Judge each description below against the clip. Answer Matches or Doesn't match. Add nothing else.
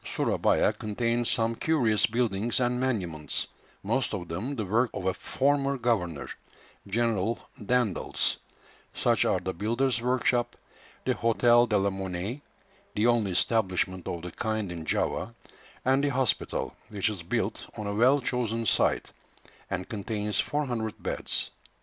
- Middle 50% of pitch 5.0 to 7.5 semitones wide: Doesn't match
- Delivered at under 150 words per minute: Matches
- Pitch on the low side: Matches